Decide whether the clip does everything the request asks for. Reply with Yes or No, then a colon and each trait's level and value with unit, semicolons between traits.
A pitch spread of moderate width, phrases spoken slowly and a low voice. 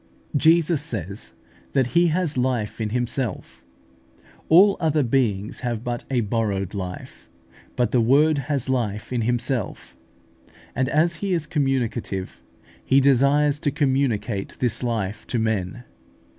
Yes: average, 4.6 semitones; slow, 130 wpm; low, 125 Hz